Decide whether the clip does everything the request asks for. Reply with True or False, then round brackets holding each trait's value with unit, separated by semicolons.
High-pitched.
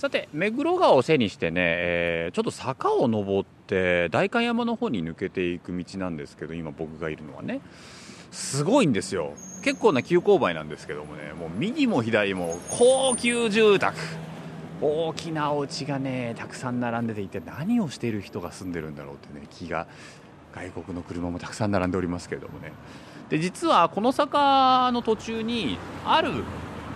False (115 Hz)